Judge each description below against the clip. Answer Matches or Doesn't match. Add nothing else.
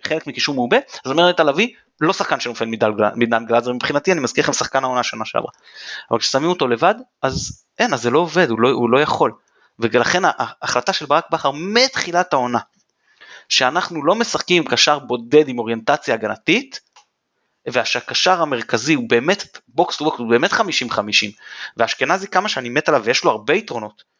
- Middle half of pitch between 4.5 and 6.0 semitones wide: Matches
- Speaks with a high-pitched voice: Doesn't match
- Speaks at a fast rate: Matches